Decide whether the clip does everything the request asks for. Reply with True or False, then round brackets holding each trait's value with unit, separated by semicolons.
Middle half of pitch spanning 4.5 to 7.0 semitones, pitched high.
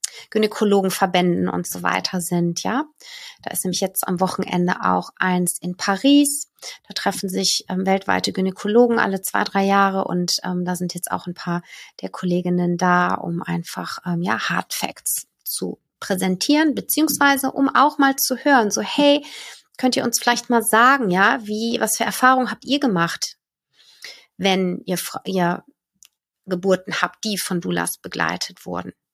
True (5.3 semitones; 195 Hz)